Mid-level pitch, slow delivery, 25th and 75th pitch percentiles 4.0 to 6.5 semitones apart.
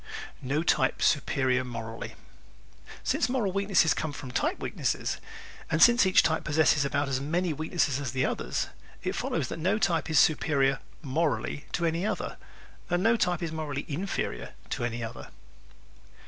No: medium, 155 Hz; average, 160 wpm; average, 4.5 semitones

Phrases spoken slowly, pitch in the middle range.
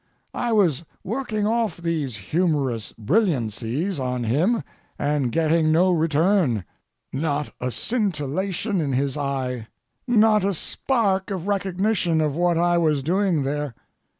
Yes: slow, 125 wpm; medium, 165 Hz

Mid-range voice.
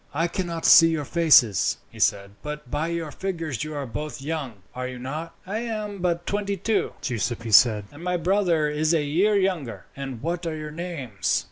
Yes: medium, 155 Hz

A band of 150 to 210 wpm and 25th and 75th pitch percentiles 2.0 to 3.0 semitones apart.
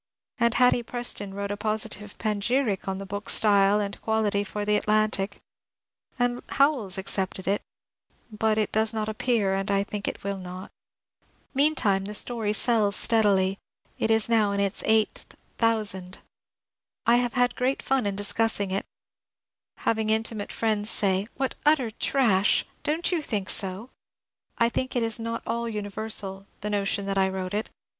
Yes: average, 170 wpm; narrow, 2.5 semitones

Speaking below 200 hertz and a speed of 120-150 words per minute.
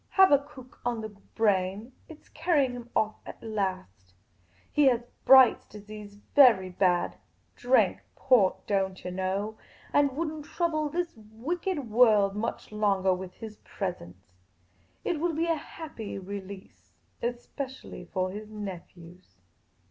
No: high, 215 Hz; average, 140 wpm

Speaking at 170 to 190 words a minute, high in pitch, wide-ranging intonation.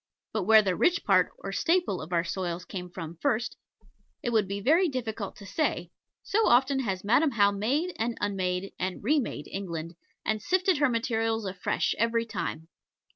Yes: average, 180 wpm; high, 215 Hz; wide, 5.8 semitones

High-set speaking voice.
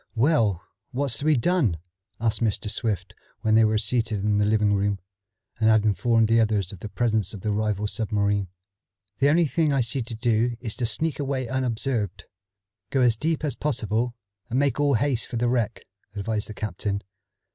No: low, 115 Hz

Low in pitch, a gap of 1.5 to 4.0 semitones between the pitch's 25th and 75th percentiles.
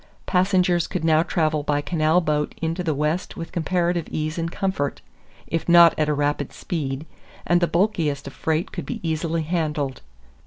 No: medium, 160 Hz; narrow, 2.4 semitones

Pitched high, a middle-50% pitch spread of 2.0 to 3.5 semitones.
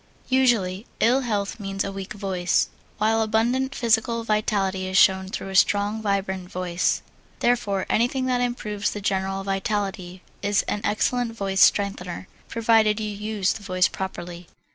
Yes: high, 205 Hz; average, 2.7 semitones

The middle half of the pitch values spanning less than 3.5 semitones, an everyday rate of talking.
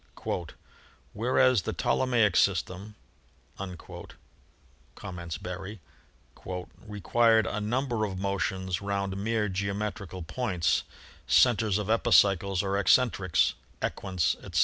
No: average, 2.9 semitones; slow, 95 wpm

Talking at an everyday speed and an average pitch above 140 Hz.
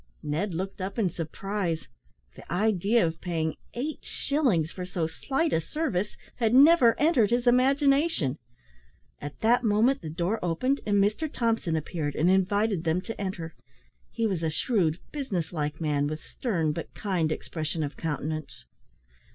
Yes: average, 155 wpm; high, 190 Hz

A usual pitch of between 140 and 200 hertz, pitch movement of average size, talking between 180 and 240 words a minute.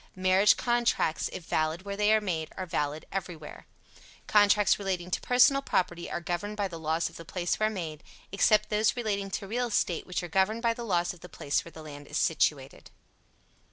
Yes: medium, 185 Hz; average, 4.0 semitones; average, 200 wpm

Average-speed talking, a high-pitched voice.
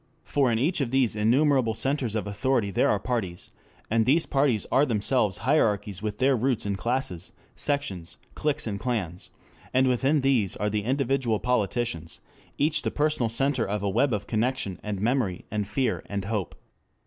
No: average, 170 wpm; low, 115 Hz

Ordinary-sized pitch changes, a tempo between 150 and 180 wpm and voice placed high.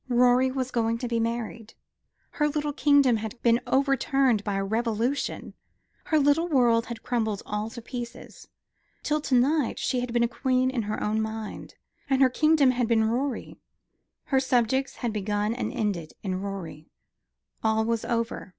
Yes: average, 3.1 semitones; average, 170 wpm; high, 235 Hz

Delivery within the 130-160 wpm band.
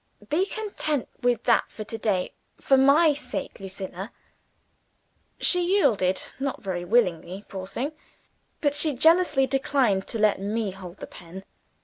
Yes: average, 140 wpm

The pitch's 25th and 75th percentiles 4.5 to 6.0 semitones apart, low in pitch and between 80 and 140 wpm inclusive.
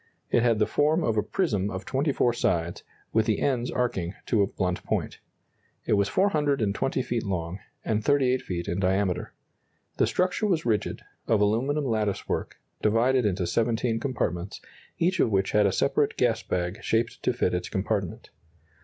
No: average, 4.9 semitones; low, 110 Hz; average, 170 wpm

